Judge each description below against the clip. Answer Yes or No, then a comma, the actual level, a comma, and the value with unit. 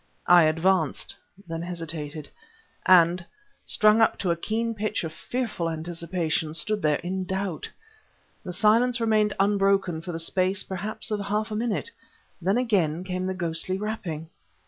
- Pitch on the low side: No, medium, 185 Hz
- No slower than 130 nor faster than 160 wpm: Yes, average, 145 wpm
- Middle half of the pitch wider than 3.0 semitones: Yes, average, 4.2 semitones